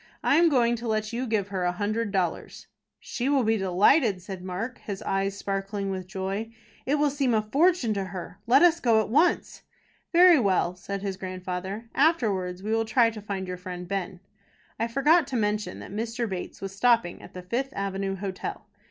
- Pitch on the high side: Yes, high, 210 Hz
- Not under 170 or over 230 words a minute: Yes, average, 195 wpm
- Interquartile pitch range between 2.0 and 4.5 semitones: Yes, average, 4.0 semitones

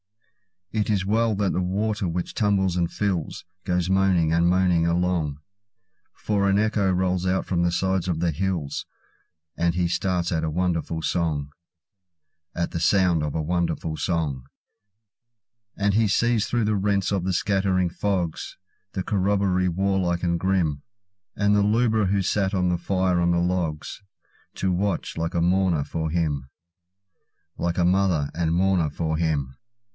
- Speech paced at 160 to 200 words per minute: No, average, 140 wpm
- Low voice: Yes, very low, 90 Hz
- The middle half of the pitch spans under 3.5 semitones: Yes, average, 2.8 semitones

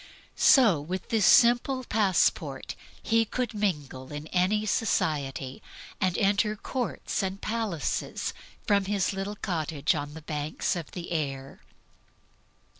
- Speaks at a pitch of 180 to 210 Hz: Yes, medium, 185 Hz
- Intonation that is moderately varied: No, wide, 6.0 semitones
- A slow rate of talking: Yes, slow, 120 wpm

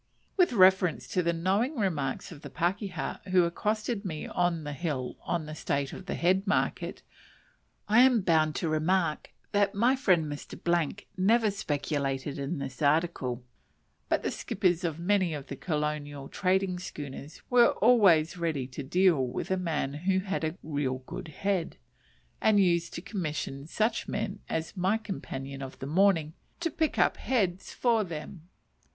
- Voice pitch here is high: No, medium, 175 Hz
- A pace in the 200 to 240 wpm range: No, average, 160 wpm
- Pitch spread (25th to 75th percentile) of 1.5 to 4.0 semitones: No, average, 4.7 semitones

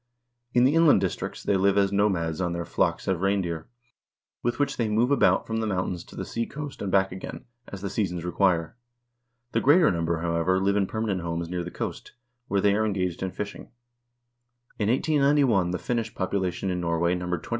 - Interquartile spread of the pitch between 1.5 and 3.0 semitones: No, average, 3.7 semitones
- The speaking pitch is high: No, very low, 95 Hz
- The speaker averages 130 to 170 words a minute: No, average, 195 wpm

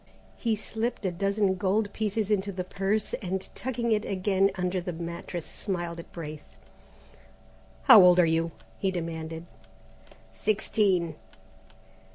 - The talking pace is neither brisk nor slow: No, slow, 130 wpm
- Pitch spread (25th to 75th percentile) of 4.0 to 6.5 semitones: No, average, 3.4 semitones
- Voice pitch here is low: No, high, 190 Hz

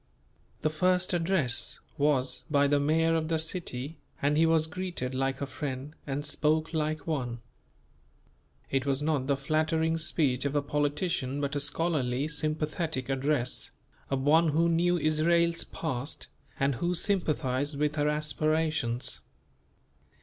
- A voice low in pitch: No, medium, 150 Hz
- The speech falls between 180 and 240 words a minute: No, average, 140 wpm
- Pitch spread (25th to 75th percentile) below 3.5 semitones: Yes, average, 2.7 semitones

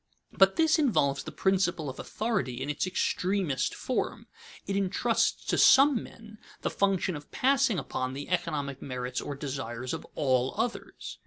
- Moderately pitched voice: Yes, medium, 180 Hz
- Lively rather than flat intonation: Yes, wide, 7.7 semitones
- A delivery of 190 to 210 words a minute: No, average, 155 wpm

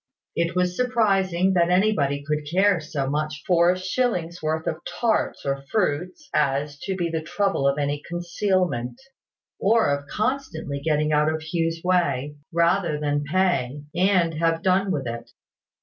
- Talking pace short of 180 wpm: Yes, average, 160 wpm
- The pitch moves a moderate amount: Yes, average, 4.0 semitones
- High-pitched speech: No, medium, 170 Hz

